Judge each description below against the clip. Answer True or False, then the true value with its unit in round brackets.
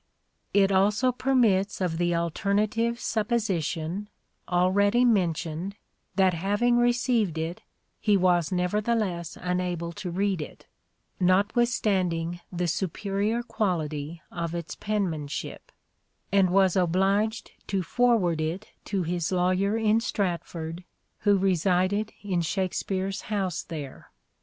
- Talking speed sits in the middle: False (110 wpm)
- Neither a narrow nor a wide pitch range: True (3.4 semitones)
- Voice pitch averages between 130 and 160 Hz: False (190 Hz)